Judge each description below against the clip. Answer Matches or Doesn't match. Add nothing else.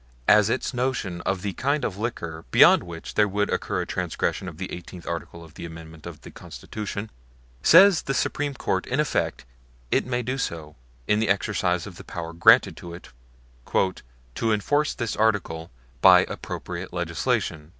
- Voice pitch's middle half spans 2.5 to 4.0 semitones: Doesn't match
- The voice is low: Matches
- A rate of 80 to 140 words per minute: Doesn't match